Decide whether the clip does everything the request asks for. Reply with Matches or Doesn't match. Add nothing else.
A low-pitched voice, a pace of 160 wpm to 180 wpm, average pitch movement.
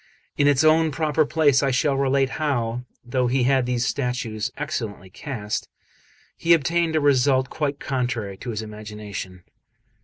Doesn't match